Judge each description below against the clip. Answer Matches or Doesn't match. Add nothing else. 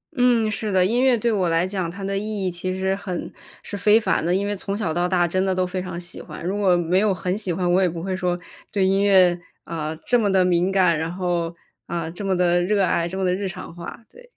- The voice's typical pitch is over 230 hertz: Doesn't match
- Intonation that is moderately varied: Doesn't match